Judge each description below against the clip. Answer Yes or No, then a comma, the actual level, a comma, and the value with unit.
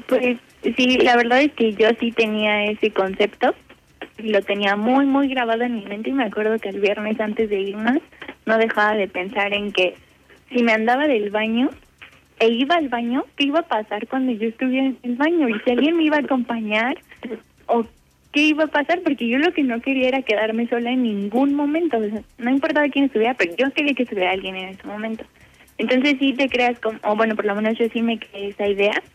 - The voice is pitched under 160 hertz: No, high, 235 Hz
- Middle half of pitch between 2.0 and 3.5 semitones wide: No, average, 4.0 semitones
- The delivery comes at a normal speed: No, fast, 220 wpm